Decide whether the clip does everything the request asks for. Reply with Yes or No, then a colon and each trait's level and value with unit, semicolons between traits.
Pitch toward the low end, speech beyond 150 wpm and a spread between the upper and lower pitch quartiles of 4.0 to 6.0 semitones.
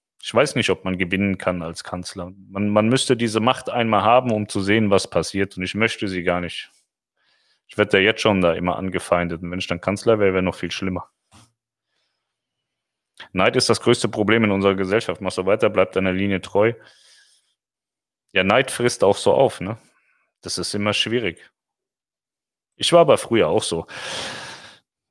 No: low, 100 Hz; average, 185 wpm; average, 3.1 semitones